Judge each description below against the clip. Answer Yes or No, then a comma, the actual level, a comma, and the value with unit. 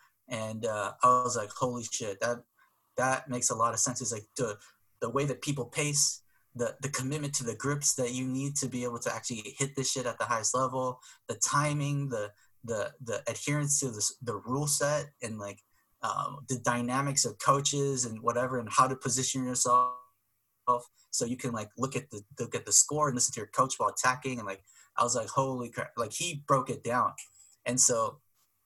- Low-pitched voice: Yes, low, 125 Hz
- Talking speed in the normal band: No, fast, 210 wpm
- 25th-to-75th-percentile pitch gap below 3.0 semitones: Yes, narrow, 2.4 semitones